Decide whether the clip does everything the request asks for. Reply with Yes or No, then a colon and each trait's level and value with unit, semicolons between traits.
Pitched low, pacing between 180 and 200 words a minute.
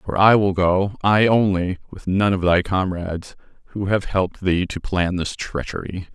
Yes: very low, 95 Hz; average, 185 wpm